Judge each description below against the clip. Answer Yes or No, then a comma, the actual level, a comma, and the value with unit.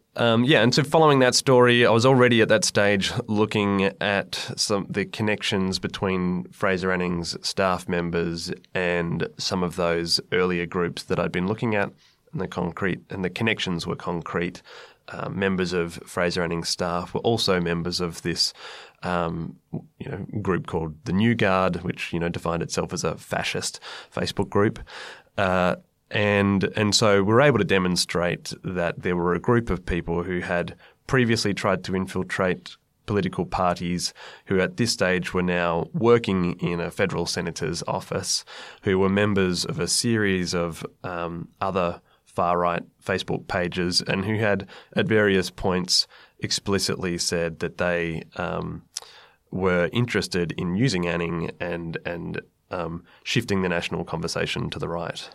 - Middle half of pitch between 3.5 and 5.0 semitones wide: No, average, 2.9 semitones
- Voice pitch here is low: Yes, very low, 90 Hz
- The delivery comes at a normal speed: Yes, average, 160 wpm